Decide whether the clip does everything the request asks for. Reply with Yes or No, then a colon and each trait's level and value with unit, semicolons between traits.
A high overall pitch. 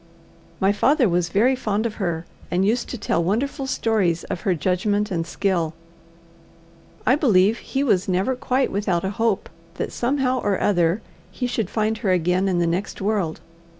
Yes: high, 200 Hz